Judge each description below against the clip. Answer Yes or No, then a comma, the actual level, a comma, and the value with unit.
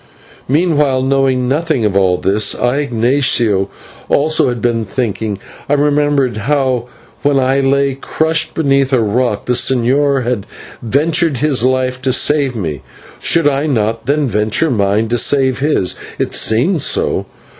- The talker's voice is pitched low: Yes, low, 130 Hz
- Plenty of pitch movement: No, average, 3.9 semitones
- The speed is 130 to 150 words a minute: Yes, average, 145 wpm